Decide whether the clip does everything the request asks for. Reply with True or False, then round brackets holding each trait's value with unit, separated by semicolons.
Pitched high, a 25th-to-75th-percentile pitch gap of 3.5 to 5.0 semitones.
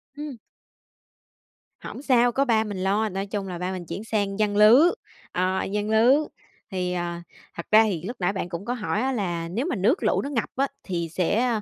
True (210 Hz; 4.3 semitones)